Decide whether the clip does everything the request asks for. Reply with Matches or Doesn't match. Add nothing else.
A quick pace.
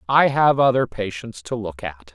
Doesn't match